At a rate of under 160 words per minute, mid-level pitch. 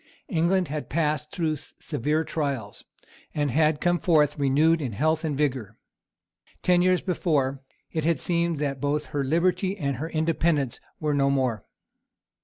Yes: average, 150 wpm; medium, 150 Hz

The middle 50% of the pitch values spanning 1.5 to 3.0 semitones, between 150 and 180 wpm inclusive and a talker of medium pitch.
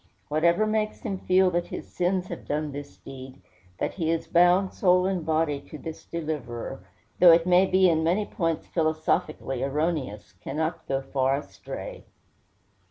No: average, 3.9 semitones; average, 160 wpm; medium, 165 Hz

